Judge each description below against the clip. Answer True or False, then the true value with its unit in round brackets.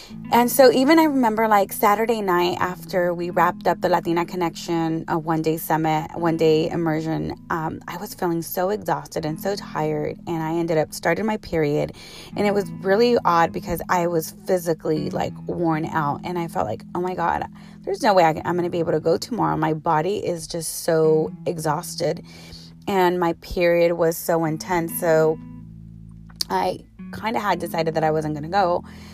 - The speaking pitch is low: False (170 Hz)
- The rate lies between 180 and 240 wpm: True (190 wpm)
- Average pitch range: False (2.2 semitones)